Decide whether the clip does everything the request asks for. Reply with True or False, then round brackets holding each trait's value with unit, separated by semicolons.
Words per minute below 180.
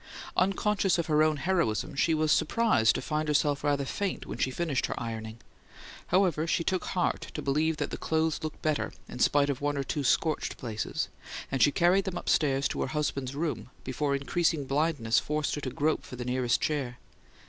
False (195 wpm)